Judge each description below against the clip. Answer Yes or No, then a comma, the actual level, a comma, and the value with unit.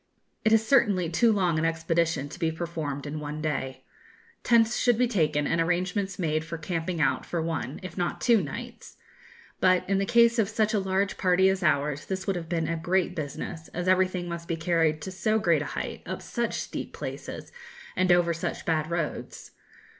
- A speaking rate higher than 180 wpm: Yes, average, 200 wpm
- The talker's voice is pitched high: No, medium, 175 Hz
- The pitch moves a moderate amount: Yes, average, 3.1 semitones